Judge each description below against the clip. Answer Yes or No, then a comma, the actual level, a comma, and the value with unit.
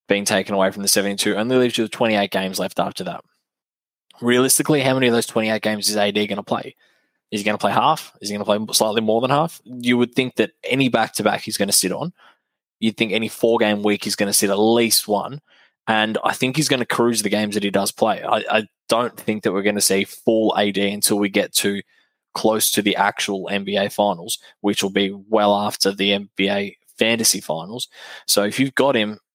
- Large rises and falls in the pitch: No, narrow, 2.4 semitones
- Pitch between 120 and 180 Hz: No, low, 105 Hz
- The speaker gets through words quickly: Yes, fast, 230 wpm